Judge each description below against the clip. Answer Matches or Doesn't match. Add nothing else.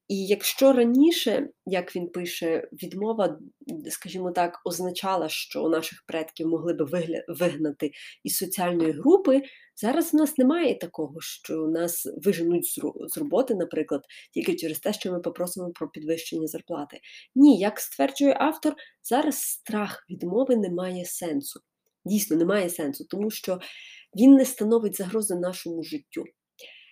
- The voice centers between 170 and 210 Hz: Matches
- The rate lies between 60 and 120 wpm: Doesn't match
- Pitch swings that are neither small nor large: Doesn't match